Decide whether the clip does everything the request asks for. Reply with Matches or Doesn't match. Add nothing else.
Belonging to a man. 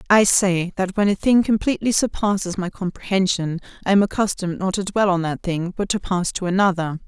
Doesn't match